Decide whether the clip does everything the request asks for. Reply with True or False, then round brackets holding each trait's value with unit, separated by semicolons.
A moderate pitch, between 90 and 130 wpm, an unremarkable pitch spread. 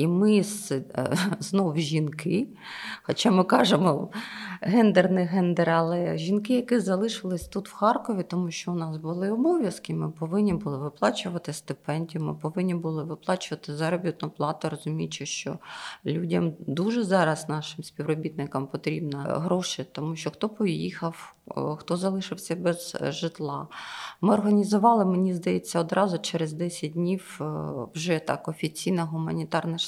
True (170 Hz; 125 wpm; 3.3 semitones)